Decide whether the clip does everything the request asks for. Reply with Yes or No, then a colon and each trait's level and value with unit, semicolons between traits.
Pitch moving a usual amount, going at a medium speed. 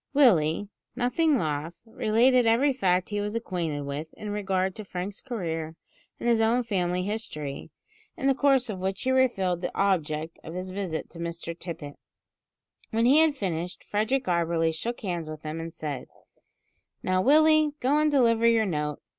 No: wide, 6.3 semitones; average, 170 wpm